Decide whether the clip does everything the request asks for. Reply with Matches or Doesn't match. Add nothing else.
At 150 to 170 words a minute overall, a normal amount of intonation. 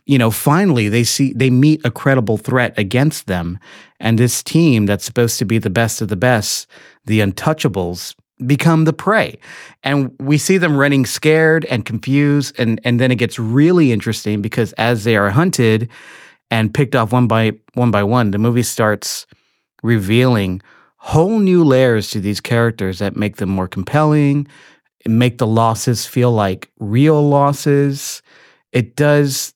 Matches